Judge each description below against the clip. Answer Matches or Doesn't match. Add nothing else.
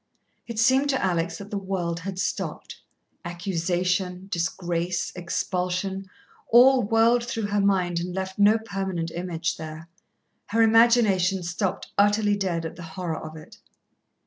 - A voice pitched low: Doesn't match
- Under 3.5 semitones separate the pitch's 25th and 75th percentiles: Matches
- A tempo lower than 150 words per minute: Matches